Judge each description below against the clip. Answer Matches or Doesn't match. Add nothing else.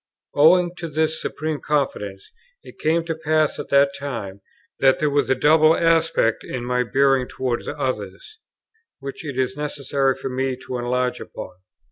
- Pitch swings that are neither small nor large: Matches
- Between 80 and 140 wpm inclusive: Doesn't match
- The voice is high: Doesn't match